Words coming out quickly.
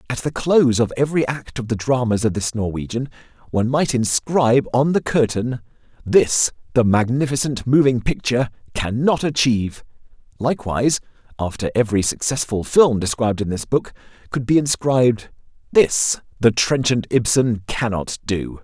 No: average, 140 wpm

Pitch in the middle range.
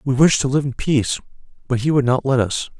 No: low, 130 Hz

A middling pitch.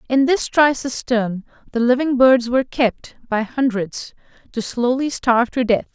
No: high, 245 Hz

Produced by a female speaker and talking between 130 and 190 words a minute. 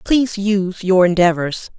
Yes: female; slow, 135 wpm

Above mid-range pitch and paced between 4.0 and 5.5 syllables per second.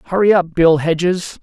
No: medium, 175 Hz; 5.1 syllables/s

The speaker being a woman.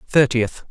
No: male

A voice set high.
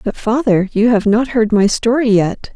Yes: high, 220 Hz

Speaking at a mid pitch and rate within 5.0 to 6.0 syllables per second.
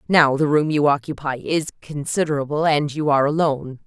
Yes: medium, 145 Hz; 5.7 syllables/s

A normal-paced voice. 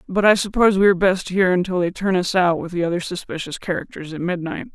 No: fast, 240 wpm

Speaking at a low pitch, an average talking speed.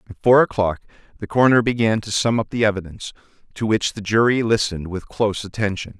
Yes: low, 110 Hz; average, 190 wpm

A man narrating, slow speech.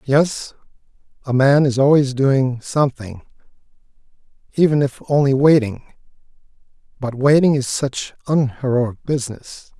Yes: male; slow, 105 wpm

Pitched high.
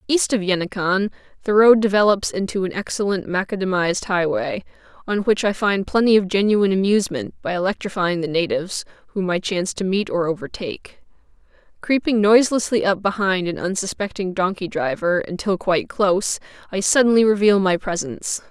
Yes: high, 195 Hz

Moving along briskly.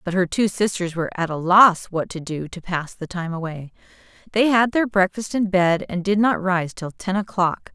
Yes: fast, 225 wpm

